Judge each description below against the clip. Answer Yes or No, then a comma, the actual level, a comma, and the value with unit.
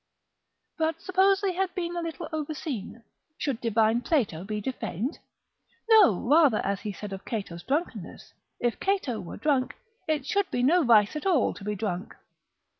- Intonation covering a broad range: Yes, wide, 7.9 semitones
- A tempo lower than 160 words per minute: No, average, 165 wpm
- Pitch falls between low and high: No, very high, 265 Hz